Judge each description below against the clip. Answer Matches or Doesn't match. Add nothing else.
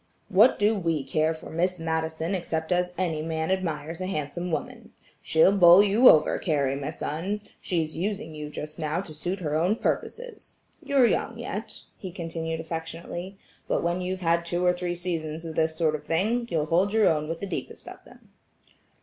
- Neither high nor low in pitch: Matches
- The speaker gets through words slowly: Doesn't match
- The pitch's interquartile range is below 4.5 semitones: Matches